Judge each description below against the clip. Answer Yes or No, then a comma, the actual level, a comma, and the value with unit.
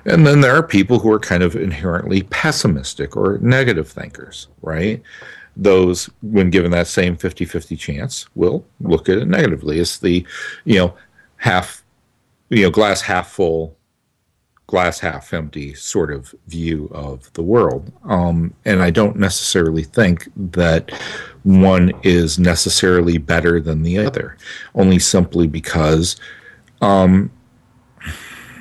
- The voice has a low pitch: Yes, very low, 90 Hz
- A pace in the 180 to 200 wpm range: No, slow, 135 wpm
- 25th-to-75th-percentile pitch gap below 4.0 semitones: Yes, narrow, 2.5 semitones